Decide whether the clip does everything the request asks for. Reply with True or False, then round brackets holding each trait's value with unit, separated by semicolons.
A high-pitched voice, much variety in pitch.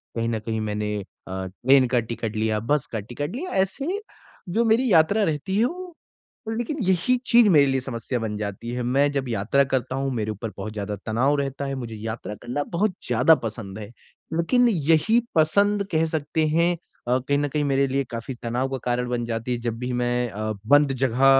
False (130 Hz; 5.7 semitones)